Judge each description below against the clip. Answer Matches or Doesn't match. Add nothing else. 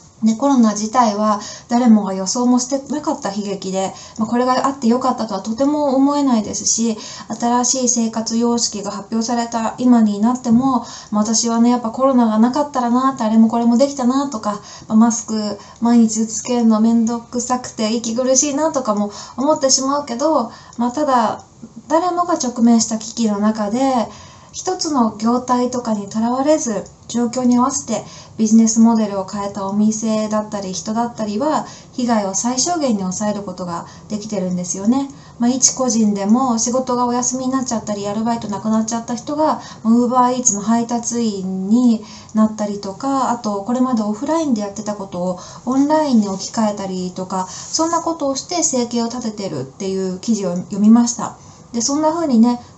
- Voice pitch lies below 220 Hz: Doesn't match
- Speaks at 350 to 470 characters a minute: Matches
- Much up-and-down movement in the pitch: Doesn't match